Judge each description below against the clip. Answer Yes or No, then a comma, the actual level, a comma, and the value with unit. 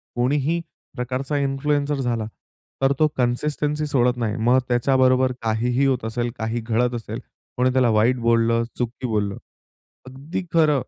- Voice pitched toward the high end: No, low, 125 Hz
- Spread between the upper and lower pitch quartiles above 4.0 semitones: No, average, 2.8 semitones